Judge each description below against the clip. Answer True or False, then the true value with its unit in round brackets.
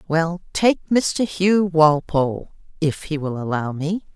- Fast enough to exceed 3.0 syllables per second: False (2.9 syllables/s)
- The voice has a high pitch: False (165 Hz)